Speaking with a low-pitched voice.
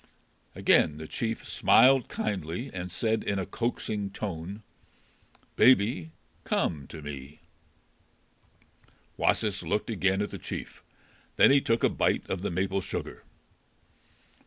Yes: very low, 95 Hz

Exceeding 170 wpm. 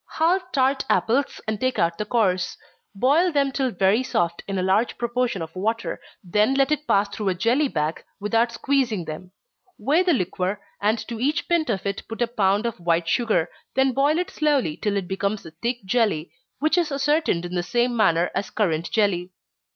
Yes: average, 200 wpm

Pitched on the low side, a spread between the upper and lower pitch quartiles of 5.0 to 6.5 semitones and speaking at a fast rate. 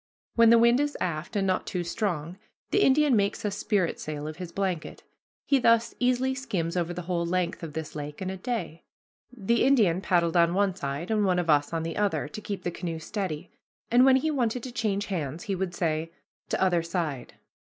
No: medium, 185 Hz; average, 5.3 semitones; fast, 210 wpm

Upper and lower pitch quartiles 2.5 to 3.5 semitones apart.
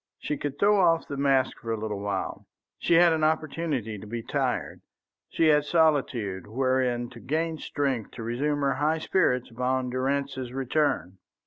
No: average, 4.4 semitones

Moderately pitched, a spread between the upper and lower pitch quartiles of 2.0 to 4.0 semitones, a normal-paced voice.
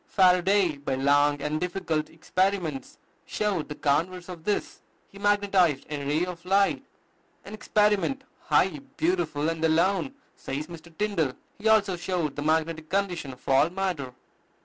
No: medium, 175 Hz; average, 4.5 semitones; average, 145 wpm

